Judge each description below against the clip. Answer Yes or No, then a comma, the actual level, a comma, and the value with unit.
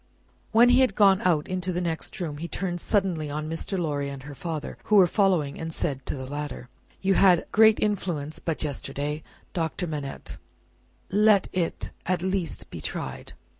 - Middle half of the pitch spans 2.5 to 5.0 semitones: Yes, average, 4.5 semitones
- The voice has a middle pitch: Yes, medium, 170 Hz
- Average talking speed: Yes, average, 175 wpm